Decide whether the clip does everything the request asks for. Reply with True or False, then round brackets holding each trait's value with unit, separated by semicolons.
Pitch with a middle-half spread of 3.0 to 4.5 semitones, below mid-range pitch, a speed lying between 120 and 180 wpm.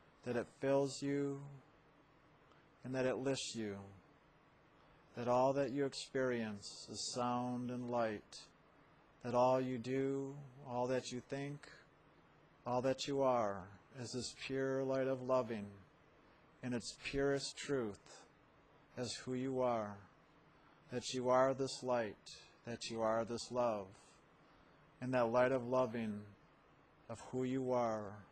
False (2.5 semitones; 125 Hz; 135 wpm)